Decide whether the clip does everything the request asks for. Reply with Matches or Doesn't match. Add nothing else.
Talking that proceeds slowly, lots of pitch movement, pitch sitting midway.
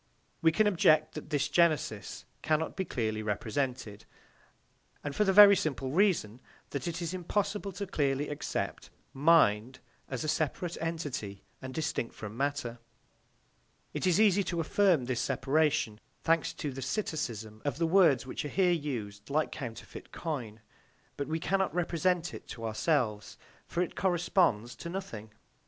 Doesn't match